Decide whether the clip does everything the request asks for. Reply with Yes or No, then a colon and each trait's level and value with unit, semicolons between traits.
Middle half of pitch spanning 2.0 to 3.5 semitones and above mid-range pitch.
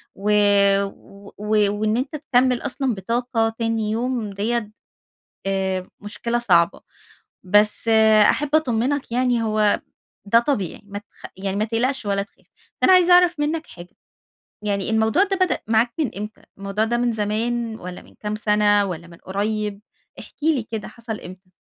Yes: average, 3.0 semitones; high, 220 Hz